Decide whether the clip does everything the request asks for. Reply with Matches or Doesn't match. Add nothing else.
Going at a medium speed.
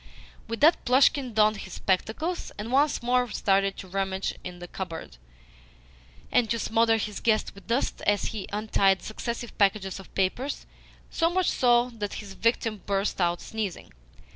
Matches